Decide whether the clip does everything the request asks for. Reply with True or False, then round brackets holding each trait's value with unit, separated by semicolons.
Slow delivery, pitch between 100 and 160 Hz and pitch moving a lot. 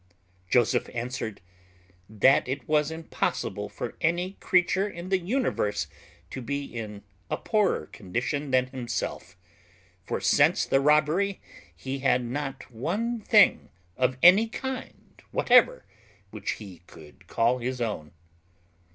True (125 wpm; 135 Hz; 6.9 semitones)